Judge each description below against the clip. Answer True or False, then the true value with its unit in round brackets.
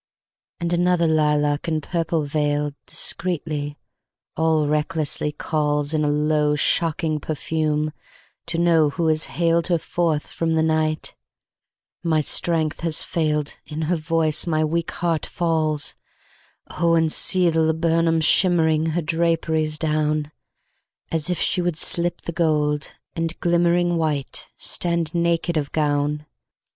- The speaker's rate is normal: False (115 wpm)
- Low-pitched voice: False (160 Hz)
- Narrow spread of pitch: True (1.8 semitones)